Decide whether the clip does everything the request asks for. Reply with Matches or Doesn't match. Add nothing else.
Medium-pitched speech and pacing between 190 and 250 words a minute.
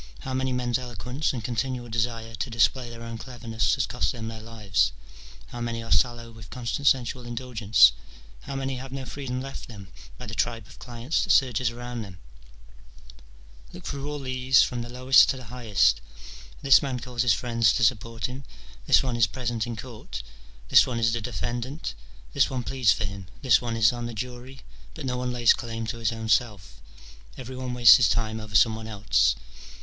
Doesn't match